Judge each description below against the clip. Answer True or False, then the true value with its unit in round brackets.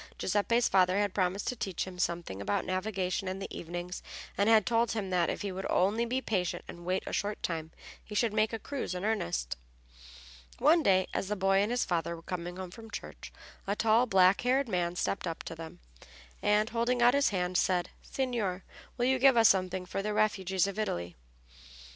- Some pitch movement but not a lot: True (3.7 semitones)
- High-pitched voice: True (195 Hz)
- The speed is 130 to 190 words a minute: False (205 wpm)